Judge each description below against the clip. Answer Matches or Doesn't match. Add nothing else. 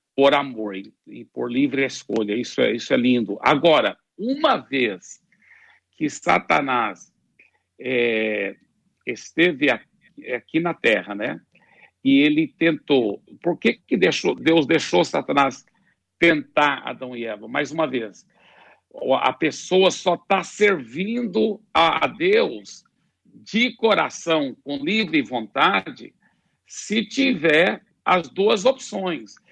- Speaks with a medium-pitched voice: Matches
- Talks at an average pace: Doesn't match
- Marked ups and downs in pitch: Matches